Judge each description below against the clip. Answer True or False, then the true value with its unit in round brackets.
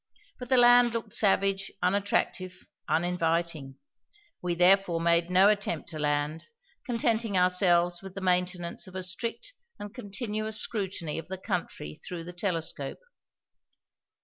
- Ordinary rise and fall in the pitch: True (3.2 semitones)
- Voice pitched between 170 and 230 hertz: True (185 Hz)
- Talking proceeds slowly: True (130 wpm)